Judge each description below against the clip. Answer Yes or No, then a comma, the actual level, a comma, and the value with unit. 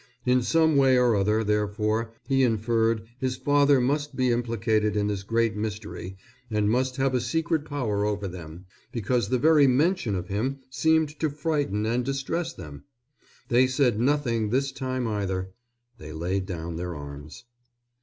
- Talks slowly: No, average, 160 wpm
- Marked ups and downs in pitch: No, average, 4.6 semitones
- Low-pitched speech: Yes, low, 115 Hz